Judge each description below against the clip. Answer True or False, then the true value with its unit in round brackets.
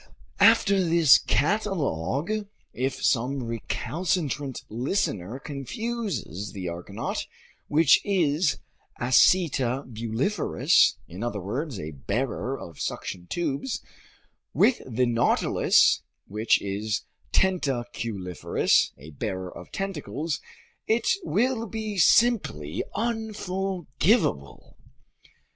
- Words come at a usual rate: False (85 wpm)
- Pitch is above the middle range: False (135 Hz)